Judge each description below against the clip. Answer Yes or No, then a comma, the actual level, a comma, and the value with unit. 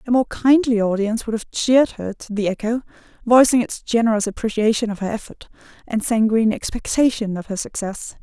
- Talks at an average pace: Yes, average, 175 wpm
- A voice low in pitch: No, high, 225 Hz